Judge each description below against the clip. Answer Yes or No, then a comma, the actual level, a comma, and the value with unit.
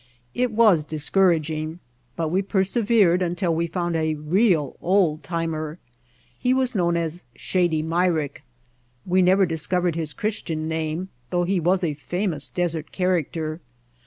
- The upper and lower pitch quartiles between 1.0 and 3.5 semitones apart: Yes, average, 3.0 semitones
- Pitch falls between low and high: Yes, medium, 170 Hz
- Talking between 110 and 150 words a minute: Yes, slow, 135 wpm